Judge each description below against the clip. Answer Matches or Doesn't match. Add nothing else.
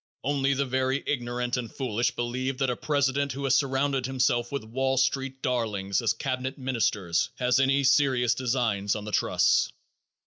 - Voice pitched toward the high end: Doesn't match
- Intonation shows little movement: Matches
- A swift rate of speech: Doesn't match